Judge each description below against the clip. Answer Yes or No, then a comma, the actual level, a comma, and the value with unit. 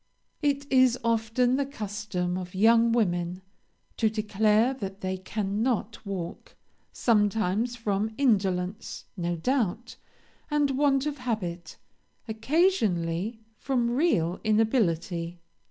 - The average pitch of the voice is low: No, high, 220 Hz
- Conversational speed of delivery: No, slow, 105 wpm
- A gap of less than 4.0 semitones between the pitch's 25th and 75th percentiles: No, average, 4.8 semitones